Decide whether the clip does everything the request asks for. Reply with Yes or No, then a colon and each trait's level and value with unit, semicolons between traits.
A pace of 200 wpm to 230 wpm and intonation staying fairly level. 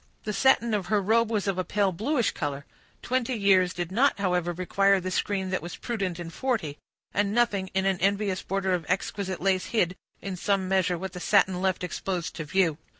Yes: fast, 205 wpm; narrow, 2.3 semitones